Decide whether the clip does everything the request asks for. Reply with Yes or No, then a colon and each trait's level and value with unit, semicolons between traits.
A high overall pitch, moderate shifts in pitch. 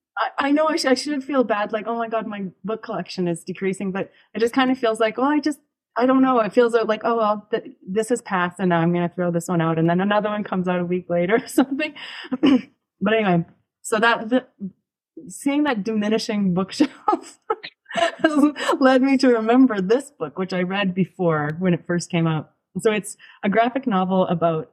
No: high, 220 Hz; wide, 6.0 semitones